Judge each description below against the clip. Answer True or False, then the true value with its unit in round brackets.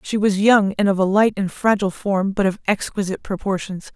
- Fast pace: True (215 wpm)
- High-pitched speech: True (195 Hz)